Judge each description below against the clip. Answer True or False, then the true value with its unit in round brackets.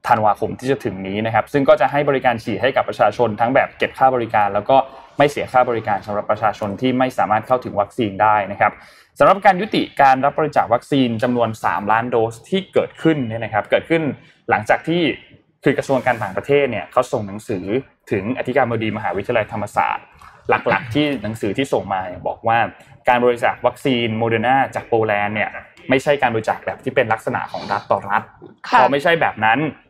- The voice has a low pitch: True (125 Hz)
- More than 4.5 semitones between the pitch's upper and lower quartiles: False (3.6 semitones)